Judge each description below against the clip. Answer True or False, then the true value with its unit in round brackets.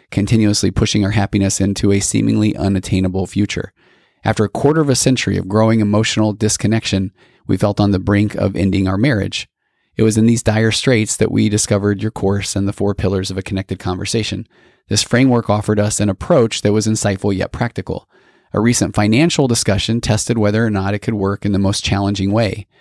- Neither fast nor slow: True (195 wpm)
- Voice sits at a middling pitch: False (105 Hz)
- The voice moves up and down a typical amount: False (2.0 semitones)